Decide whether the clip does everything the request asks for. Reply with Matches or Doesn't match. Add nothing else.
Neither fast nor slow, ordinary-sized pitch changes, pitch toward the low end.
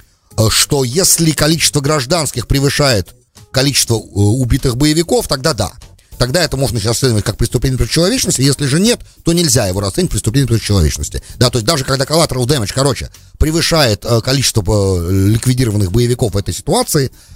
Doesn't match